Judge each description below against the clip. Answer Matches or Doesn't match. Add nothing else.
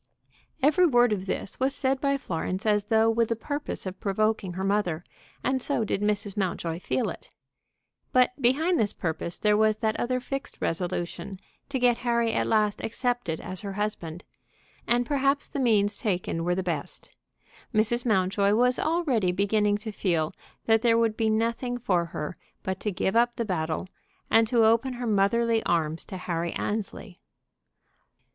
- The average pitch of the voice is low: Doesn't match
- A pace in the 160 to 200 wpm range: Matches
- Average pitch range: Matches